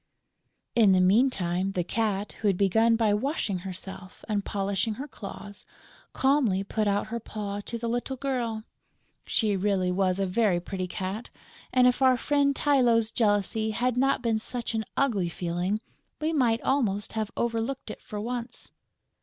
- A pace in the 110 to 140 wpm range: No, average, 160 wpm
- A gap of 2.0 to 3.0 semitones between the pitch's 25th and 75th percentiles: No, average, 3.7 semitones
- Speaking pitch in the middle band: No, high, 215 Hz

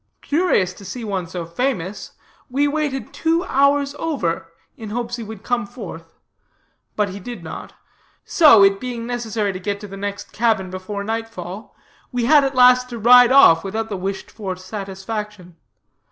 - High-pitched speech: Yes, high, 220 Hz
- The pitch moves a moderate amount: Yes, average, 4.4 semitones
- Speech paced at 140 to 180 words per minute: Yes, average, 170 wpm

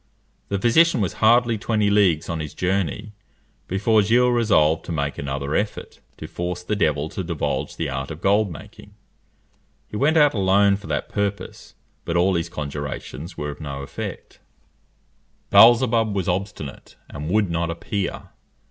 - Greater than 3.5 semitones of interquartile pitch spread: Yes, average, 5.2 semitones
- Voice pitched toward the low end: Yes, very low, 95 Hz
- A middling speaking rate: Yes, average, 155 wpm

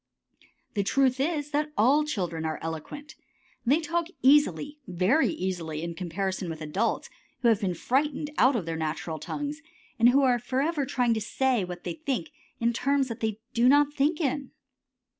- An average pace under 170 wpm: No, average, 175 wpm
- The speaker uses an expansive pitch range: Yes, wide, 7.8 semitones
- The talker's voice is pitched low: No, high, 245 Hz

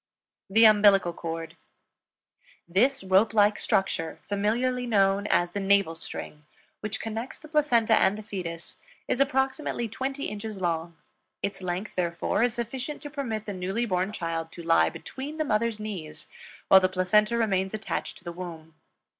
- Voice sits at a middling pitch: No, high, 205 Hz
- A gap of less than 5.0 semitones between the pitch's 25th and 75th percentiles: Yes, average, 4.2 semitones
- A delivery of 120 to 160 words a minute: Yes, average, 155 wpm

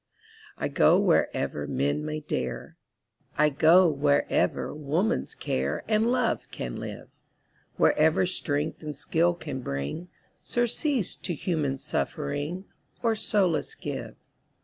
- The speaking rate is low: Yes, slow, 115 wpm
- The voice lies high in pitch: No, medium, 155 Hz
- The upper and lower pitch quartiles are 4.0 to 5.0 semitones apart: Yes, average, 4.6 semitones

